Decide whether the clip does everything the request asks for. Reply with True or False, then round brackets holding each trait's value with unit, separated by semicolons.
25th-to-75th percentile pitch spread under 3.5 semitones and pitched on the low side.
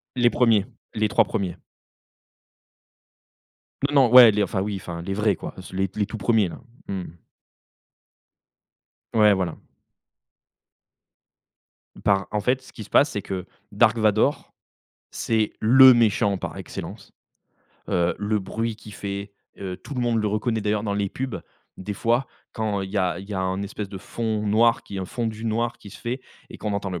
True (2.7 semitones; 105 Hz)